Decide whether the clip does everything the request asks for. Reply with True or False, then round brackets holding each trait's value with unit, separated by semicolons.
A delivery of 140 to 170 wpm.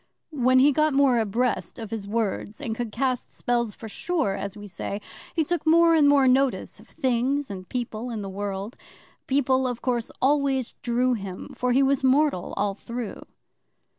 False (180 wpm)